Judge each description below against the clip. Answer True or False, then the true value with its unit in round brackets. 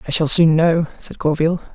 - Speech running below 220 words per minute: True (205 wpm)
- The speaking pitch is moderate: True (160 Hz)